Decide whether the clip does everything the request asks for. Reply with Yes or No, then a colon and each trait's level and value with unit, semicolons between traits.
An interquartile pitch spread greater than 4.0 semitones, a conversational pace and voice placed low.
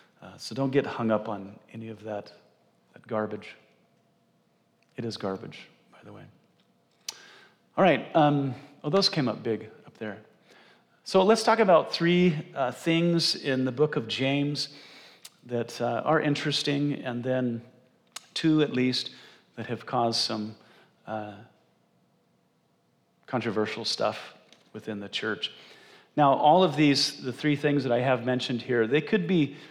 Yes: average, 4.7 semitones; average, 150 wpm; low, 130 Hz